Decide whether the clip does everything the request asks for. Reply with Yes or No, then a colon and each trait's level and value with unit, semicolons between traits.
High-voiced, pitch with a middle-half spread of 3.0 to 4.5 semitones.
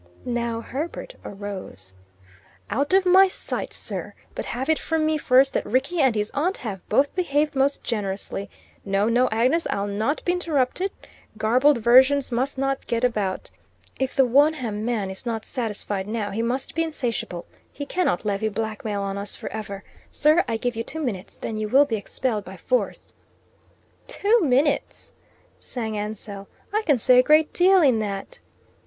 No: high, 245 Hz; wide, 5.4 semitones